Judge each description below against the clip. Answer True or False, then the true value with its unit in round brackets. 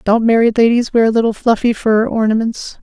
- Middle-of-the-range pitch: False (225 Hz)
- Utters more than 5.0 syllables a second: True (5.2 syllables/s)